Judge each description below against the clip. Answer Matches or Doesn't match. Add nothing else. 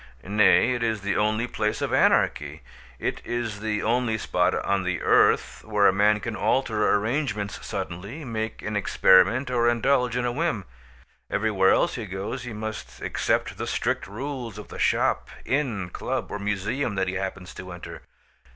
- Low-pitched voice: Matches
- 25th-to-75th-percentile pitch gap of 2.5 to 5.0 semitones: Matches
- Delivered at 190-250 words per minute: Doesn't match